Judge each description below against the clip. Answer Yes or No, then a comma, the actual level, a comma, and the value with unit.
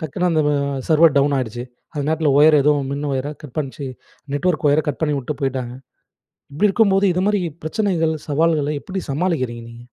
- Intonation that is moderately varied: Yes, average, 3.3 semitones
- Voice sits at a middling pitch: Yes, medium, 150 Hz